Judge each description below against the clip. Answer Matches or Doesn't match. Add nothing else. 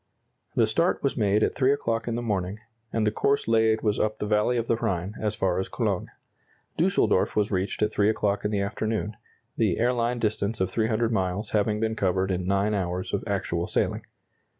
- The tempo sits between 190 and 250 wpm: Matches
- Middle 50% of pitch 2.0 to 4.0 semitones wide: Matches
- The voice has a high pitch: Doesn't match